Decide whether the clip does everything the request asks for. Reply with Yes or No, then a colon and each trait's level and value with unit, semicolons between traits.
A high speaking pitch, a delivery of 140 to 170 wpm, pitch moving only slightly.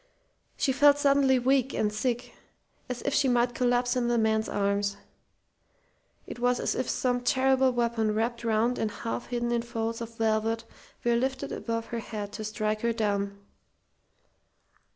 Yes: high, 235 Hz; average, 160 wpm; narrow, 2.3 semitones